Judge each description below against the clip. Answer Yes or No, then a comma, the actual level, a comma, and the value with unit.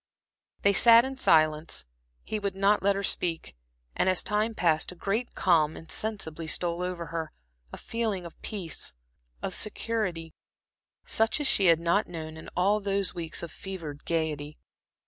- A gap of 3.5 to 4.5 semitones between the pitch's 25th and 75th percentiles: Yes, average, 4.0 semitones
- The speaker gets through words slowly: No, average, 160 wpm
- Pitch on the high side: No, medium, 180 Hz